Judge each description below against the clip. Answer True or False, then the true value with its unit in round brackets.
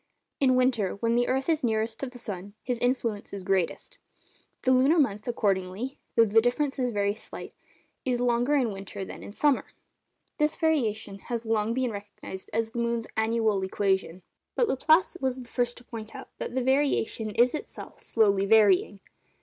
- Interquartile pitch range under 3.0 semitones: False (3.9 semitones)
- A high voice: True (230 Hz)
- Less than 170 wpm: False (175 wpm)